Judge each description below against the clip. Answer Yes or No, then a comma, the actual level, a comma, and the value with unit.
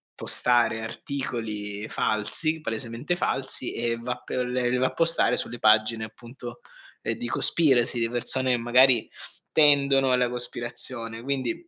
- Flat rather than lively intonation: Yes, narrow, 2.3 semitones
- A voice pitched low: Yes, low, 120 Hz